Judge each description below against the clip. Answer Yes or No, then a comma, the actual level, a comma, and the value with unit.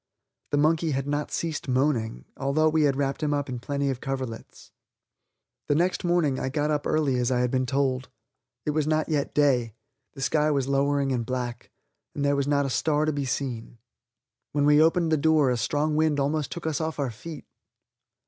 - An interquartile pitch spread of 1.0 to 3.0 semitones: Yes, average, 2.7 semitones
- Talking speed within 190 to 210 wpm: Yes, fast, 205 wpm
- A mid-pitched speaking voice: Yes, medium, 145 Hz